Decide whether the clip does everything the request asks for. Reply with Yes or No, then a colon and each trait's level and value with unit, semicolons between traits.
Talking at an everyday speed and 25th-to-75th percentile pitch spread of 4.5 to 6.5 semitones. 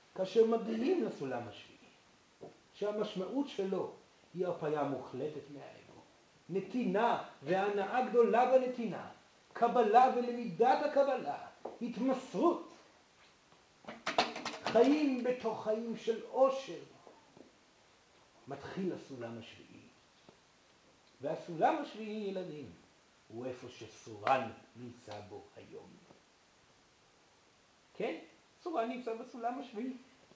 No: slow, 80 wpm; wide, 5.5 semitones